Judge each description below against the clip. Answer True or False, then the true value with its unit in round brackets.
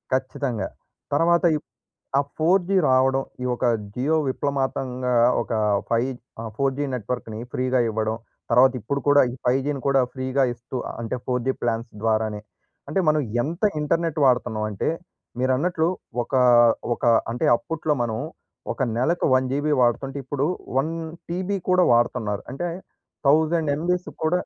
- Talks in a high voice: False (135 Hz)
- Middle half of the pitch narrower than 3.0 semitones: False (4.3 semitones)